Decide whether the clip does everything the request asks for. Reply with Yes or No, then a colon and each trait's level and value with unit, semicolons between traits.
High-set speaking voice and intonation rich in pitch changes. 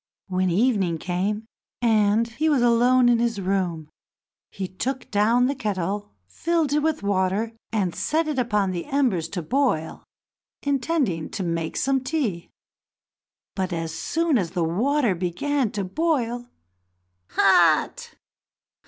Yes: high, 215 Hz; wide, 6.3 semitones